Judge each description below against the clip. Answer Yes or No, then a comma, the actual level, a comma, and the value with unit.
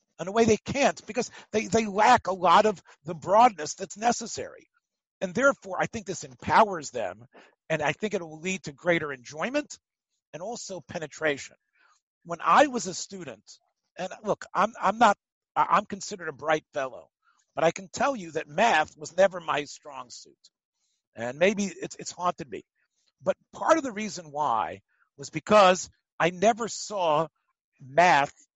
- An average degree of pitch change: No, wide, 5.8 semitones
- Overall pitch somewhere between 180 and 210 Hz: Yes, high, 190 Hz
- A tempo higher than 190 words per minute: No, average, 170 wpm